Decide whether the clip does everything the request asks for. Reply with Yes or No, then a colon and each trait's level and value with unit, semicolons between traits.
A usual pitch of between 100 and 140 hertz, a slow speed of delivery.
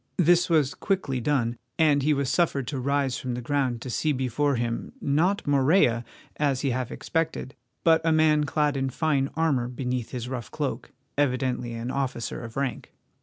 No: low, 135 Hz; average, 175 wpm